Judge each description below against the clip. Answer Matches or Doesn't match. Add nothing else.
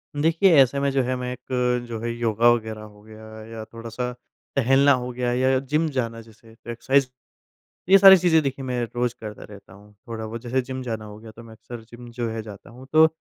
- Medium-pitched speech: Doesn't match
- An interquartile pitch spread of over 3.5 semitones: Doesn't match